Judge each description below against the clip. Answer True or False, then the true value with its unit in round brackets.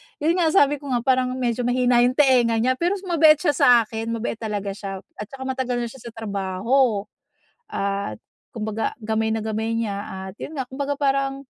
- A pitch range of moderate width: True (3.8 semitones)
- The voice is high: True (240 Hz)